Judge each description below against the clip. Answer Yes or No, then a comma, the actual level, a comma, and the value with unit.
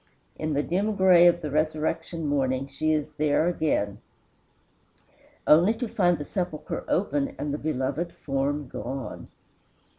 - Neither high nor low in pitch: Yes, medium, 155 Hz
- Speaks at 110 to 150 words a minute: Yes, average, 140 wpm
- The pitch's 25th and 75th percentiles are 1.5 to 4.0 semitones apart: Yes, average, 3.5 semitones